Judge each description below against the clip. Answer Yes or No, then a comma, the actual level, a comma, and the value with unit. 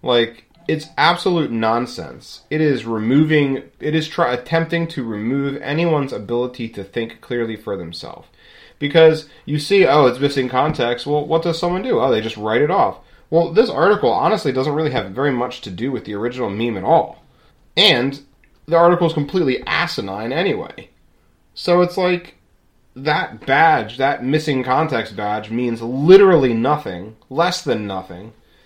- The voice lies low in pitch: Yes, low, 130 Hz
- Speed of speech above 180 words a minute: No, average, 160 wpm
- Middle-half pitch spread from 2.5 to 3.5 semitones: No, wide, 5.4 semitones